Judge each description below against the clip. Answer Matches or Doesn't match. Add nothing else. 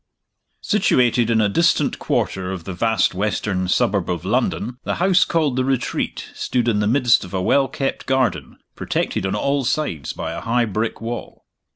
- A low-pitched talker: Matches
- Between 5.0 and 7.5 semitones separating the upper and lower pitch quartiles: Matches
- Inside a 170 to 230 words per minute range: Matches